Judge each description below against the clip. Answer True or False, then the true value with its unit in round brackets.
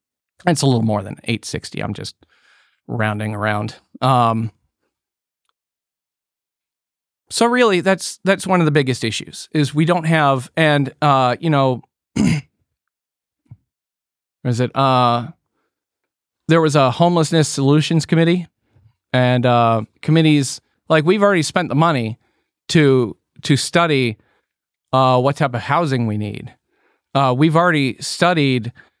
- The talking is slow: True (125 wpm)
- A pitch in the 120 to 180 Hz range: True (135 Hz)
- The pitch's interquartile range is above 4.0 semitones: True (5.2 semitones)